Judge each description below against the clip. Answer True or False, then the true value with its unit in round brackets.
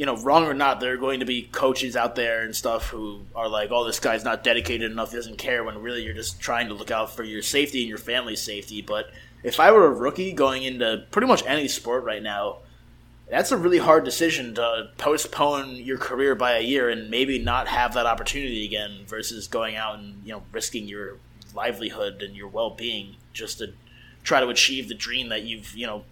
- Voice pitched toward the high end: False (115 Hz)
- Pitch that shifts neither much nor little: True (3.1 semitones)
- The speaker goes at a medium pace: False (225 wpm)